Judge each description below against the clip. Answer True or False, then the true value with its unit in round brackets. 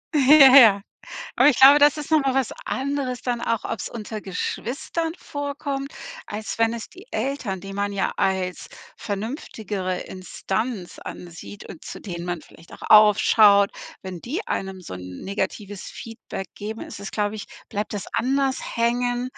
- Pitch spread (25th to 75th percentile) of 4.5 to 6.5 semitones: True (5.2 semitones)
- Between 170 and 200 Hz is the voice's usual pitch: False (220 Hz)